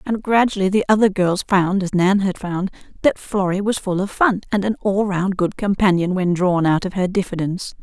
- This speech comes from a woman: Yes, female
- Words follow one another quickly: Yes, fast, 215 wpm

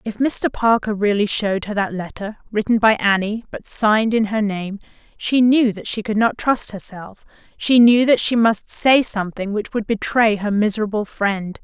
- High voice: Yes, high, 215 Hz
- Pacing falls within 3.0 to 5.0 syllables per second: Yes, 4.8 syllables/s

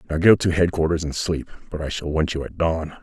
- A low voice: Yes, very low, 80 Hz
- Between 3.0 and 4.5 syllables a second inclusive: No, 5.8 syllables/s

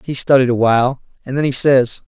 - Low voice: Yes, low, 130 Hz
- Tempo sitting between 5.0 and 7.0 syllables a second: Yes, 5.8 syllables/s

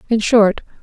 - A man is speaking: No, female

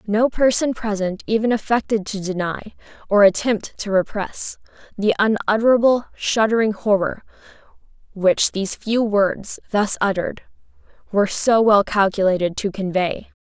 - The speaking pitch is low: No, high, 210 Hz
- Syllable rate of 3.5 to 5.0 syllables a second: Yes, 4.8 syllables/s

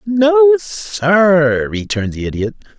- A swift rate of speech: No, slow, 110 wpm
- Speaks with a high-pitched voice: No, medium, 180 Hz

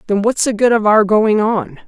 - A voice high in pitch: Yes, high, 215 Hz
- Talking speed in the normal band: No, fast, 255 wpm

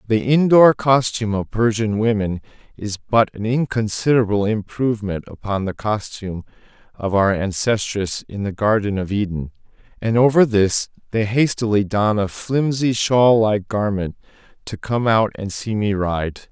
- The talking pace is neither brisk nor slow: Yes, average, 145 wpm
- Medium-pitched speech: No, low, 110 Hz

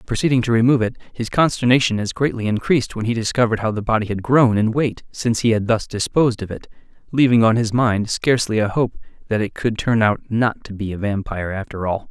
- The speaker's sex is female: No, male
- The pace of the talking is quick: Yes, fast, 225 wpm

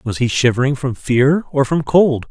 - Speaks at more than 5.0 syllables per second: No, 4.6 syllables/s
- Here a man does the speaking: Yes, male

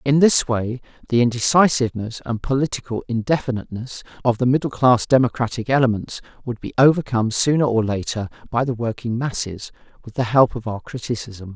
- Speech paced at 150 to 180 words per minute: Yes, average, 155 wpm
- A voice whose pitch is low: Yes, low, 120 Hz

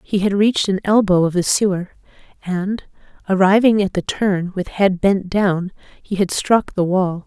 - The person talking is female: Yes, female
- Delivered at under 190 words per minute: Yes, average, 180 wpm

